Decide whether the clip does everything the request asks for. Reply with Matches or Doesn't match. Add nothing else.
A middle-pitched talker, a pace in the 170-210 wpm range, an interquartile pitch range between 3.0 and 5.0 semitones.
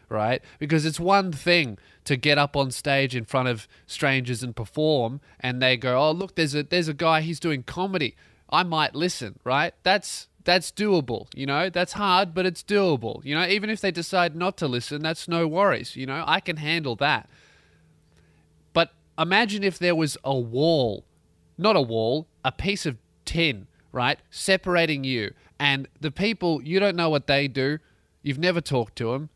Doesn't match